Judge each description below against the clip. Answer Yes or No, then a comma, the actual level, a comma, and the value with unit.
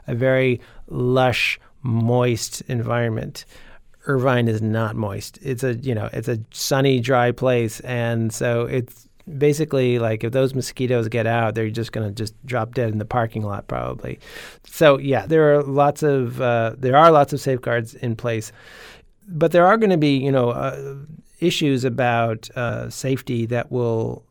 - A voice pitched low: Yes, low, 125 Hz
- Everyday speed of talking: Yes, average, 170 wpm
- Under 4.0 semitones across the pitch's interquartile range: Yes, average, 2.8 semitones